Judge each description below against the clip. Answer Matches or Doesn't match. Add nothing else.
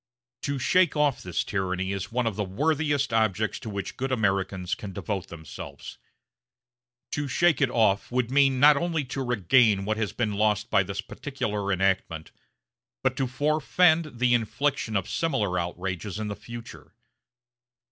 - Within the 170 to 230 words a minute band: Doesn't match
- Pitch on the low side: Matches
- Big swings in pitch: Matches